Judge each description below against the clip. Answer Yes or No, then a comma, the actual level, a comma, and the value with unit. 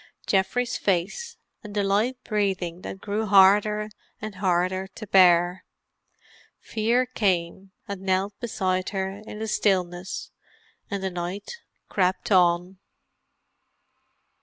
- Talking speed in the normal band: No, slow, 110 wpm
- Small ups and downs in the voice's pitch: Yes, narrow, 2.3 semitones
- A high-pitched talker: Yes, high, 195 Hz